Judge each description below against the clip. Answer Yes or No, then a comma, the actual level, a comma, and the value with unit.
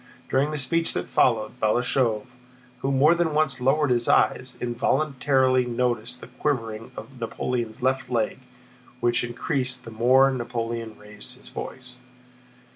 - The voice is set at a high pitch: No, low, 125 Hz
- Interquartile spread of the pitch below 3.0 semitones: Yes, narrow, 2.4 semitones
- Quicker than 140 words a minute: No, slow, 135 wpm